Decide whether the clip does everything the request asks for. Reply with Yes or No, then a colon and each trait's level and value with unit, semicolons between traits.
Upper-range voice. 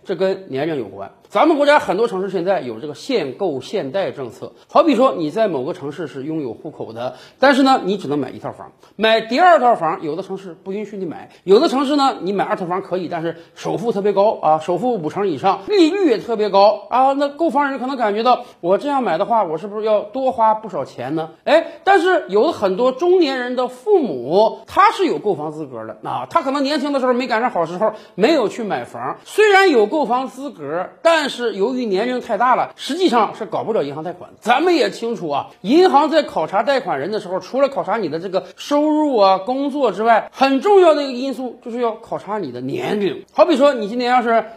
Yes: high, 240 Hz